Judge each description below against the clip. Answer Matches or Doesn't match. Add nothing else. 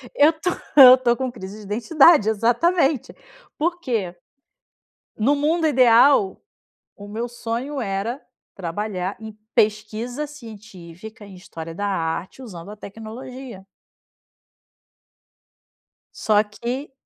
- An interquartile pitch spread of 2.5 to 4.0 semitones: Doesn't match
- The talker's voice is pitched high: Matches